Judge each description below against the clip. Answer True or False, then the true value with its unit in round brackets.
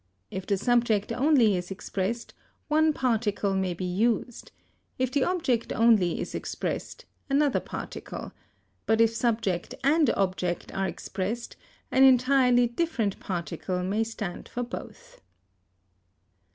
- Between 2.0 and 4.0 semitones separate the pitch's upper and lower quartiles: False (4.6 semitones)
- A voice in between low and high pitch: False (225 Hz)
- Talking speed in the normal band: False (125 wpm)